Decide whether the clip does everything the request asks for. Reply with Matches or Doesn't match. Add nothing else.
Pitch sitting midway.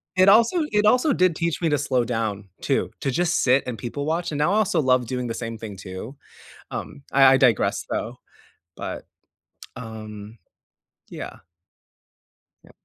Doesn't match